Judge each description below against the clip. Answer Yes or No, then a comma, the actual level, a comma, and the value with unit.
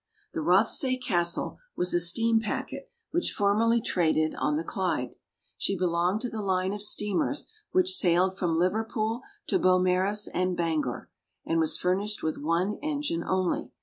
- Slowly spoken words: No, average, 150 wpm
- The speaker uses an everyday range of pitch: Yes, average, 4.2 semitones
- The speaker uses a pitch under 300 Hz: Yes, medium, 185 Hz